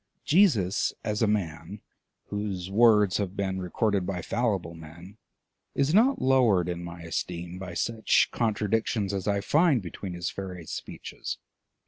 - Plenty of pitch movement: No, average, 3.9 semitones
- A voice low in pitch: Yes, low, 100 Hz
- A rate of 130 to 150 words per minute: Yes, average, 140 wpm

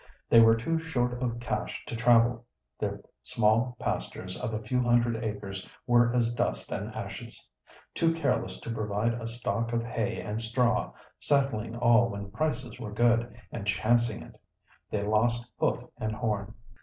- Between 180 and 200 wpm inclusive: No, average, 160 wpm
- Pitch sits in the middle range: No, low, 115 Hz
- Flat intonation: Yes, narrow, 1.9 semitones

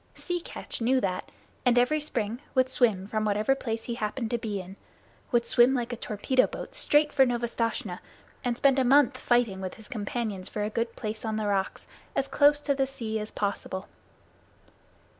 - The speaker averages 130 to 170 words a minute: No, average, 190 wpm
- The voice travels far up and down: No, average, 3.6 semitones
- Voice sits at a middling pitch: No, high, 235 Hz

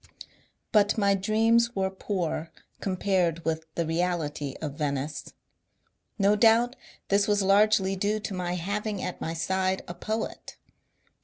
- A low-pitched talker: No, high, 190 Hz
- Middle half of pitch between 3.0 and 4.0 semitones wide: Yes, average, 3.7 semitones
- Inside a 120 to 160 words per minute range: Yes, average, 140 wpm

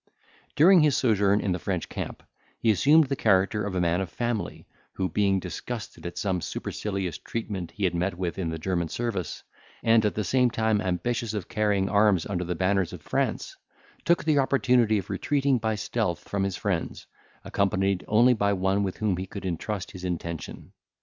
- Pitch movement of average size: Yes, average, 3.6 semitones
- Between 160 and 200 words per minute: Yes, average, 190 wpm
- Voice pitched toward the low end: Yes, low, 100 Hz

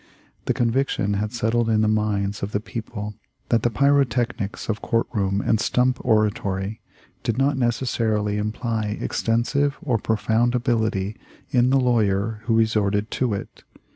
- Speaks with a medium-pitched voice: No, low, 110 Hz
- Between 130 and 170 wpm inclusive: Yes, average, 145 wpm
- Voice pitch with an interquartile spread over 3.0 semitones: No, narrow, 2.5 semitones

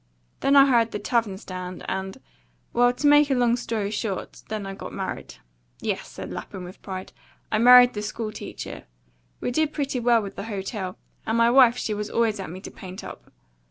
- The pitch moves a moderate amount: Yes, average, 4.0 semitones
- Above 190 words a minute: Yes, average, 200 wpm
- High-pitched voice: Yes, high, 220 Hz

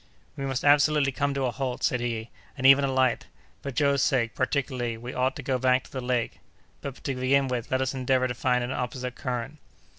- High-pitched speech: No, low, 130 Hz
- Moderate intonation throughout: No, narrow, 1.8 semitones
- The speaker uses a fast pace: Yes, fast, 215 wpm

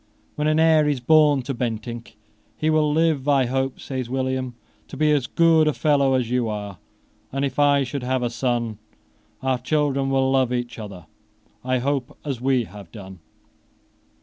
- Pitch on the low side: Yes, low, 130 Hz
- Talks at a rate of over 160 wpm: Yes, average, 175 wpm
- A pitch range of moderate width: Yes, average, 3.1 semitones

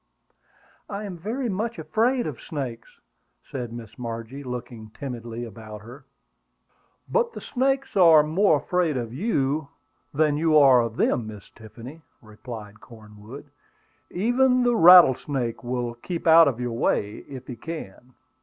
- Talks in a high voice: No, low, 135 Hz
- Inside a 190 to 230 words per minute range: No, average, 140 wpm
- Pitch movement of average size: No, wide, 6.9 semitones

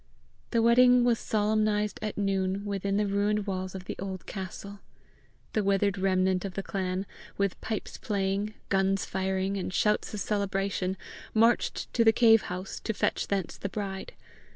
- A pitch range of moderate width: No, narrow, 1.7 semitones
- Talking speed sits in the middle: Yes, average, 160 wpm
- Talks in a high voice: Yes, high, 200 Hz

